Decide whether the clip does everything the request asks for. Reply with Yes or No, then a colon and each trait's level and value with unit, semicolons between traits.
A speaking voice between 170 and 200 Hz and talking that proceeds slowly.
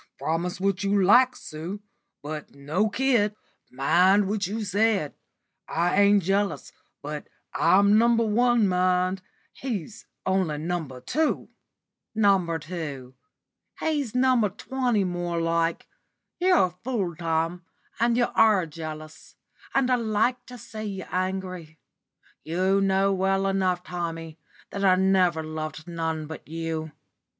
Yes: high, 190 Hz; slow, 125 wpm